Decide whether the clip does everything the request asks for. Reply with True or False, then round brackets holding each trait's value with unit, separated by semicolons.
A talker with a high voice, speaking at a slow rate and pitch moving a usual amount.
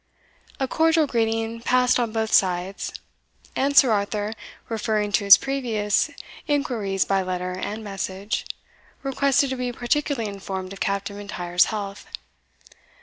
True (215 Hz; 130 wpm; 4.1 semitones)